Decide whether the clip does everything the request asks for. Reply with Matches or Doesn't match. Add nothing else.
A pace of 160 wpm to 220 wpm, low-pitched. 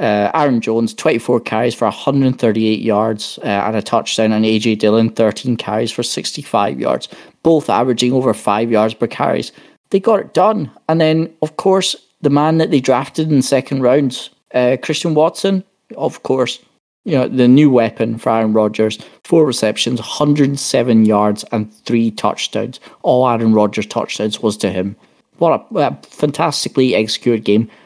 Matches